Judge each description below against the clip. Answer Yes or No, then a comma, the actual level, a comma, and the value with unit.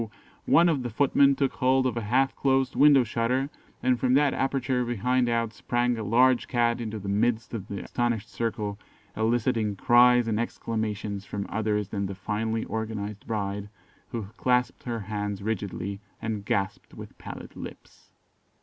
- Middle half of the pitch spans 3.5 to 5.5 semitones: No, average, 3.1 semitones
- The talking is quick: No, average, 160 wpm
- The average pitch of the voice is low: Yes, low, 115 Hz